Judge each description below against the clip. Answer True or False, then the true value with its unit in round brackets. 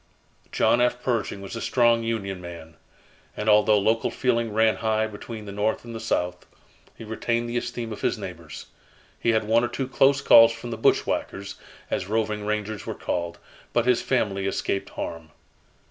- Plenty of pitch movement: False (2.9 semitones)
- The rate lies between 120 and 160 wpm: False (175 wpm)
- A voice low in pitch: True (110 Hz)